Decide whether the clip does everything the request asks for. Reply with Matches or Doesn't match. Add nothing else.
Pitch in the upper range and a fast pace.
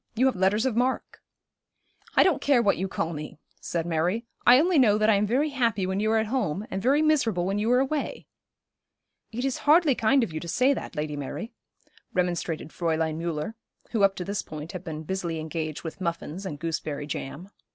Matches